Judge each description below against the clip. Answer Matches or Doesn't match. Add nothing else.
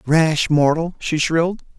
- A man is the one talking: Matches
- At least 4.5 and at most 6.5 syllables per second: Doesn't match